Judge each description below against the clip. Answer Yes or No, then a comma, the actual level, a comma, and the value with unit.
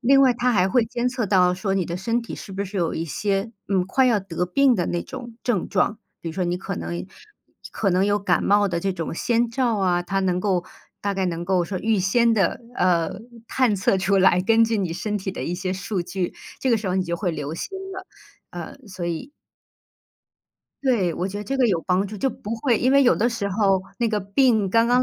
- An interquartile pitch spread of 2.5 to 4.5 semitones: Yes, average, 4.1 semitones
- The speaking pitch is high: Yes, high, 195 Hz